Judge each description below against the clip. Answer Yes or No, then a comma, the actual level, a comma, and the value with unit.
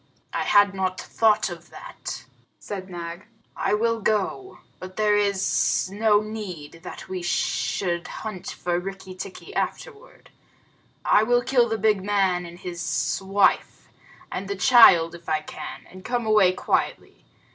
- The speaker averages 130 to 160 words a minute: Yes, average, 145 wpm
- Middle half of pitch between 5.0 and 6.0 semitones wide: No, average, 3.2 semitones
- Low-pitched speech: No, high, 195 Hz